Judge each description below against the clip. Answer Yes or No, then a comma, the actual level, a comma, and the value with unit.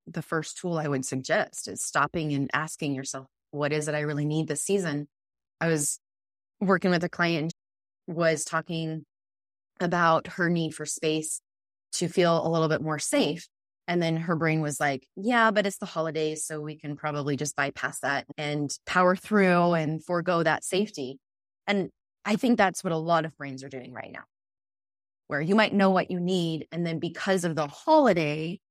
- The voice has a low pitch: No, medium, 160 Hz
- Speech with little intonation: No, average, 3.1 semitones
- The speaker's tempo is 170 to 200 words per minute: Yes, average, 190 wpm